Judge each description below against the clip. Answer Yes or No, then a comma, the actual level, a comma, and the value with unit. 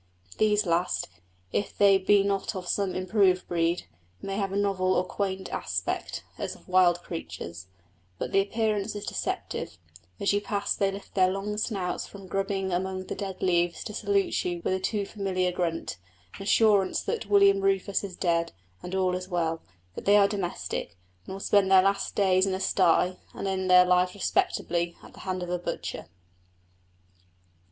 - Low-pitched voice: No, high, 190 Hz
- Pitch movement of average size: No, narrow, 1.7 semitones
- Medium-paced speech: Yes, average, 180 wpm